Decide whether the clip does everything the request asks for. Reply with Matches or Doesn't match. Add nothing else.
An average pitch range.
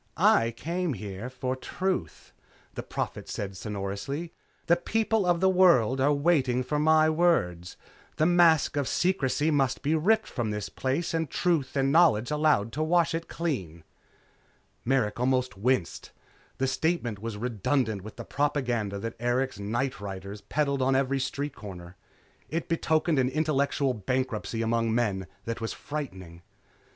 Doesn't match